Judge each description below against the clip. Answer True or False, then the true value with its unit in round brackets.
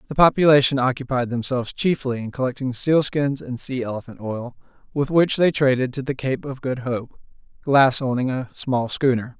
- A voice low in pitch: True (130 Hz)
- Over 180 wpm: False (170 wpm)